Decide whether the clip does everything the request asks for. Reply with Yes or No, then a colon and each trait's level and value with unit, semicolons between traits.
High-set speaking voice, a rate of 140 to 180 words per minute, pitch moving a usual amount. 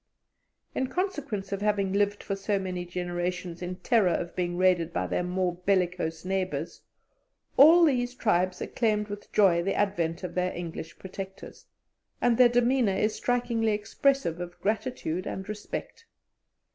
Yes: high, 195 Hz; average, 145 wpm; average, 3.8 semitones